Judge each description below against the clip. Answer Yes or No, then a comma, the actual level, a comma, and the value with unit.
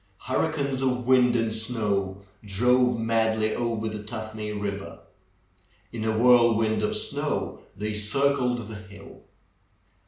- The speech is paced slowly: Yes, slow, 120 wpm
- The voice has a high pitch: No, low, 110 Hz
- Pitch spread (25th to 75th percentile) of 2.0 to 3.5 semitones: Yes, average, 2.7 semitones